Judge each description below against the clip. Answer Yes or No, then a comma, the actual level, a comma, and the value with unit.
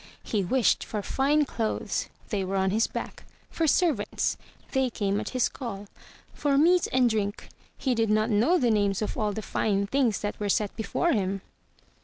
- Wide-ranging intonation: No, average, 4.5 semitones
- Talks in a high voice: Yes, high, 220 Hz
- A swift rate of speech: No, average, 185 wpm